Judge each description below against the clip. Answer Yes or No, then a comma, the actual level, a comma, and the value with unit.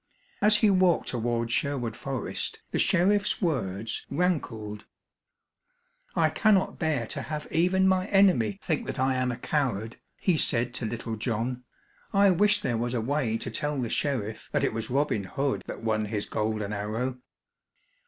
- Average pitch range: No, wide, 6.6 semitones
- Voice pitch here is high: No, low, 125 Hz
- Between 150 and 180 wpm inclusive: Yes, average, 165 wpm